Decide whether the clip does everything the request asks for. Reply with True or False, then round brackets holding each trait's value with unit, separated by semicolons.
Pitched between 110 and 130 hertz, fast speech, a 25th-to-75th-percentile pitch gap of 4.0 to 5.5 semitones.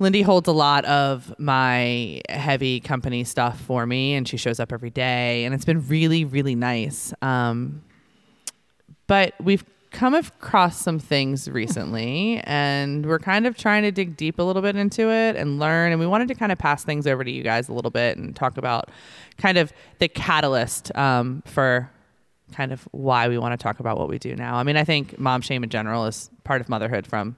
False (140 Hz; 210 wpm; 5.1 semitones)